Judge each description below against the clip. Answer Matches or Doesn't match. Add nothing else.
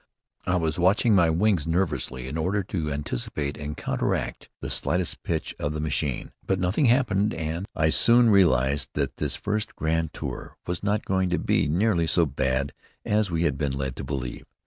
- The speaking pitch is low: Matches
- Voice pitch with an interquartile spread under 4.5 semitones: Doesn't match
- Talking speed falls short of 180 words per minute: Doesn't match